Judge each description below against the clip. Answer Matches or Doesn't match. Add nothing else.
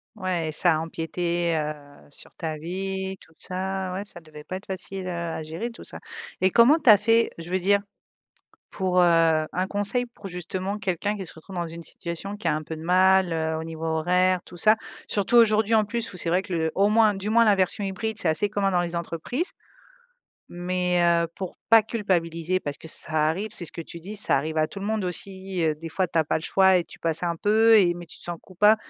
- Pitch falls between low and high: Matches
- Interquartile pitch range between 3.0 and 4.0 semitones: Matches